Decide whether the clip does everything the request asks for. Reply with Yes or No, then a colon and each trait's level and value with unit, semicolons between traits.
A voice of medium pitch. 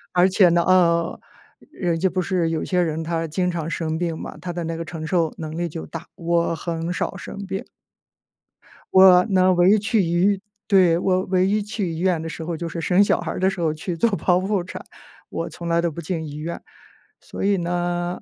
Yes: medium, 175 Hz